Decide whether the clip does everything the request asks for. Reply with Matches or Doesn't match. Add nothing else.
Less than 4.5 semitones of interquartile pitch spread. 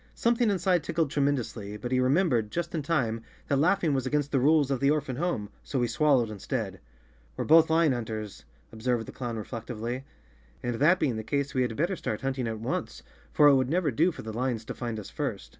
Doesn't match